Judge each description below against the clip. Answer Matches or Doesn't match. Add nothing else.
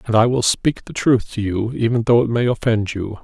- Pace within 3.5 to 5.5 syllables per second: Matches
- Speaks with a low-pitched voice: Matches